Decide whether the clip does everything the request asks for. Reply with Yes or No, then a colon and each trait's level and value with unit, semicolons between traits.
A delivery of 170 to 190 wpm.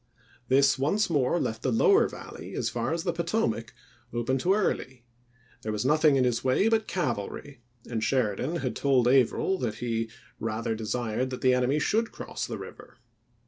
Yes: average, 180 wpm